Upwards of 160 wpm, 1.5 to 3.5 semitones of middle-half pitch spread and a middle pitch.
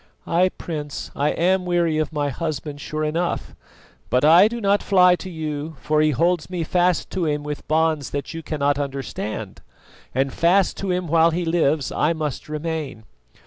Yes: average, 180 wpm; average, 3.0 semitones; medium, 160 Hz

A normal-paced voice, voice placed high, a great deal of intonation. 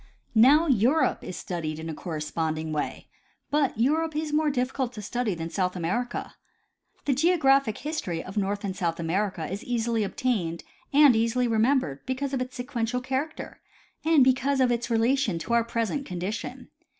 Yes: average, 160 wpm; high, 235 Hz; wide, 6.4 semitones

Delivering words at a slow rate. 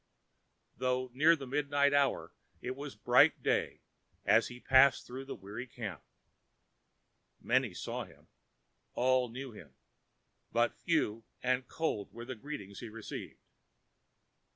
Yes: slow, 130 wpm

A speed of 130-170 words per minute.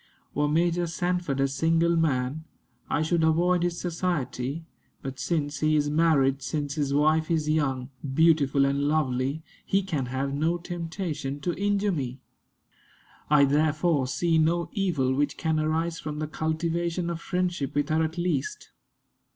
Yes: average, 150 wpm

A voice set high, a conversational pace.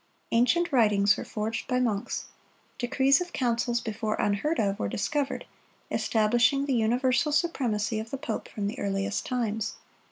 Yes: high, 230 Hz; average, 150 wpm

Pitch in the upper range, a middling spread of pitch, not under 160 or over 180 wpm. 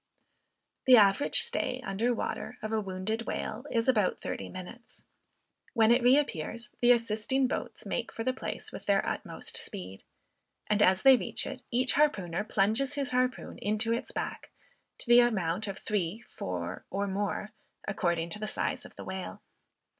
Yes: high, 215 Hz; average, 4.1 semitones; average, 165 wpm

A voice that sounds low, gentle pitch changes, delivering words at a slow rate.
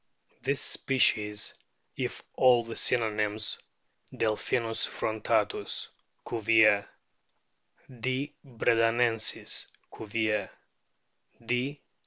Yes: low, 115 Hz; narrow, 2.2 semitones; slow, 65 wpm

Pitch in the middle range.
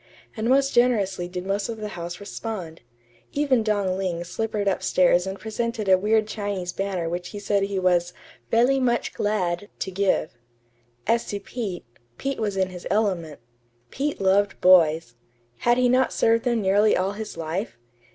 No: high, 200 Hz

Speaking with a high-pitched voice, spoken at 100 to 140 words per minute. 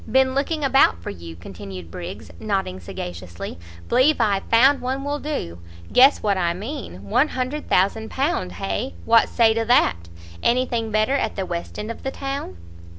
No: high, 220 Hz; average, 160 wpm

